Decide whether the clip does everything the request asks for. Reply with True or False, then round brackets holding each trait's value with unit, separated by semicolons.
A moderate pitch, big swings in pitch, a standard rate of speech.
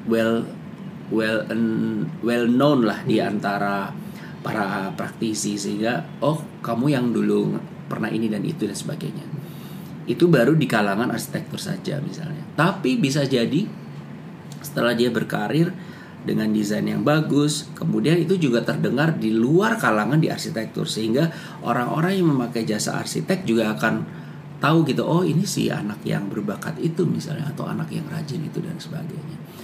False (145 Hz; 7.2 semitones; 145 wpm)